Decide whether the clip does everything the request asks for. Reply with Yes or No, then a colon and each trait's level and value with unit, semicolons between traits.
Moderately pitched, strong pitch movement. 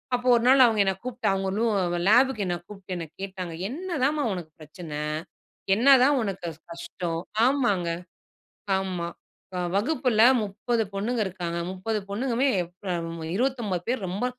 No: high, 205 Hz; wide, 5.7 semitones